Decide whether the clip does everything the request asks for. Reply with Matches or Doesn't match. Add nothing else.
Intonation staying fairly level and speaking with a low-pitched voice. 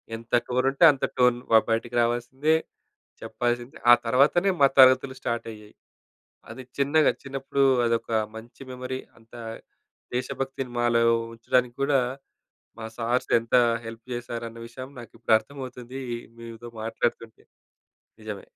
Matches